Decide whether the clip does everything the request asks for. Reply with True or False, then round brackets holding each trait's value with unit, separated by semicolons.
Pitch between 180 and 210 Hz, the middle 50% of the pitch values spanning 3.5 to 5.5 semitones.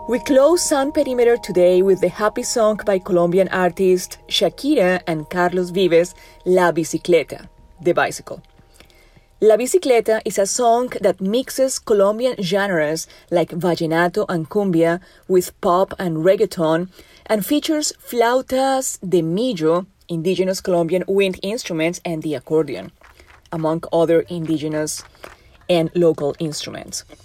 True (185 Hz; 4.6 semitones)